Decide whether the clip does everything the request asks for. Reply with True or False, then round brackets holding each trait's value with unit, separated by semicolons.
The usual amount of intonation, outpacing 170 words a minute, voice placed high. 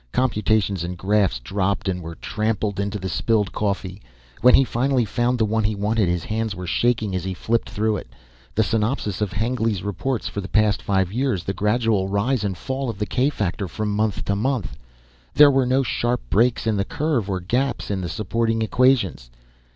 False (3.5 semitones; 195 wpm; 105 Hz)